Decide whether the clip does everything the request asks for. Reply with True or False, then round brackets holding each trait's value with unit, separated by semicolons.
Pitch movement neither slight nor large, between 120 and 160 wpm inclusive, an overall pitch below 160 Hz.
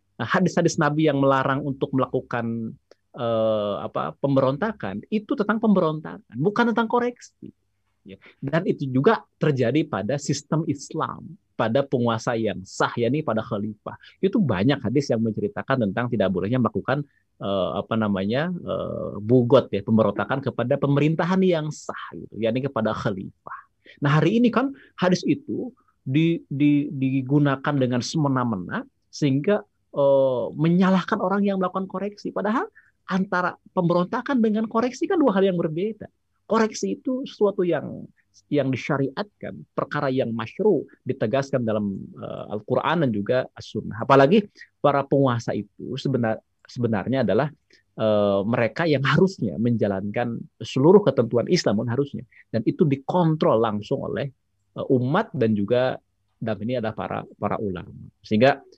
False (7.6 semitones; 130 wpm; 135 Hz)